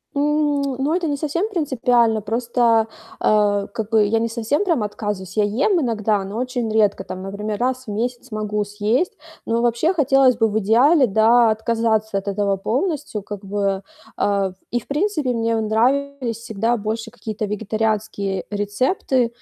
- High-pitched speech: Yes, high, 225 Hz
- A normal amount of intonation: Yes, average, 3.6 semitones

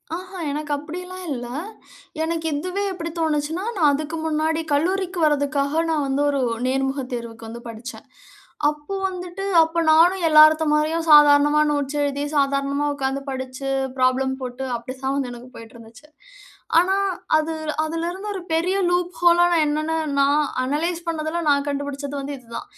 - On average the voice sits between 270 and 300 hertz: Yes, very high, 295 Hz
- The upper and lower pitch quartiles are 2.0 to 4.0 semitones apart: Yes, average, 3.3 semitones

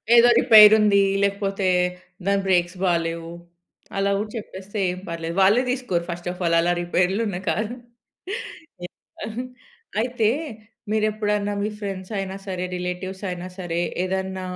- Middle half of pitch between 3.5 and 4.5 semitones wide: No, average, 2.7 semitones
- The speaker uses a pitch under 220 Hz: Yes, high, 190 Hz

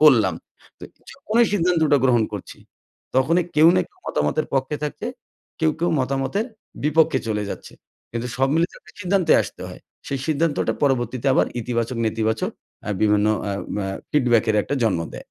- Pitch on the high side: No, low, 135 Hz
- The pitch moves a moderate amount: No, wide, 6.0 semitones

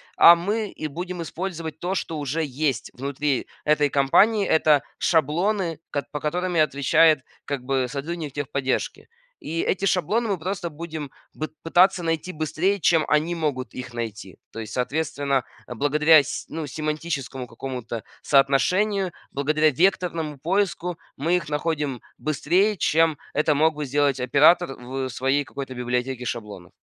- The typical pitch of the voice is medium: Yes, medium, 150 Hz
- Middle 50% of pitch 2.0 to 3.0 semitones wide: No, average, 3.8 semitones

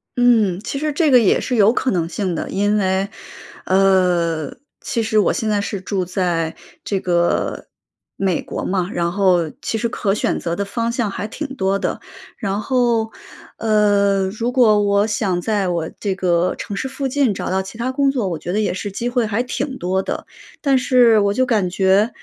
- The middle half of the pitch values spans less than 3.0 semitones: No, average, 3.8 semitones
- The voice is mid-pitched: No, high, 200 Hz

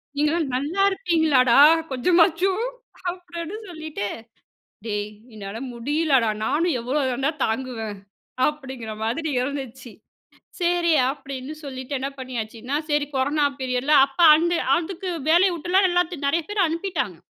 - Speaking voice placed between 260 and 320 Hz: Yes, very high, 290 Hz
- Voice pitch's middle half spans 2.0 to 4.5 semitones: No, average, 5.1 semitones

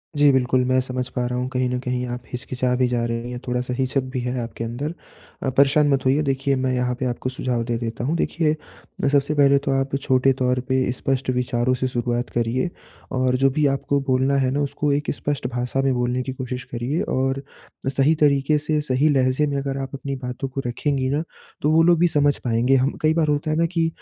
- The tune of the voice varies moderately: No, narrow, 2.2 semitones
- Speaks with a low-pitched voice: Yes, low, 130 Hz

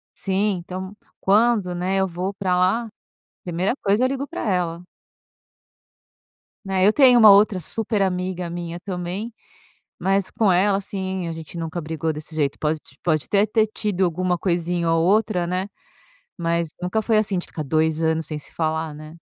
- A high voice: No, medium, 180 Hz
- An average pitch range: Yes, average, 3.2 semitones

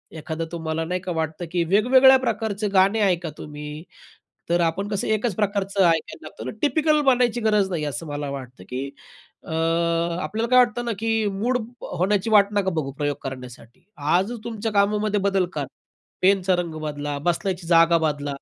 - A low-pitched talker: No, medium, 185 Hz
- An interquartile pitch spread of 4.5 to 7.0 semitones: Yes, average, 5.2 semitones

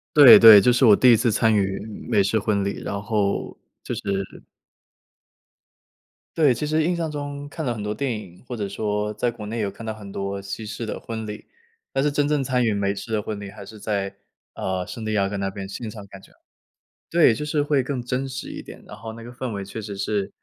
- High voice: No, low, 110 Hz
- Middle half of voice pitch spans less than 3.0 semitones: No, average, 3.8 semitones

